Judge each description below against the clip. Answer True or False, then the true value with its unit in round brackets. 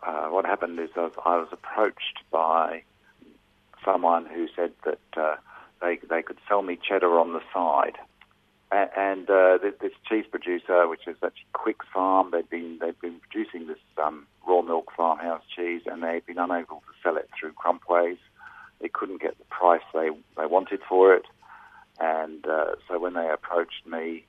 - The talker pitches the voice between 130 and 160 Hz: False (85 Hz)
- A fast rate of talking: False (185 wpm)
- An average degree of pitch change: False (2.2 semitones)